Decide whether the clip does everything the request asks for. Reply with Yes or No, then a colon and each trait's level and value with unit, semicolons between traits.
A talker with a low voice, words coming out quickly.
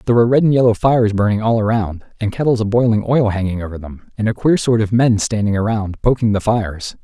Yes: low, 110 Hz; fast, 240 wpm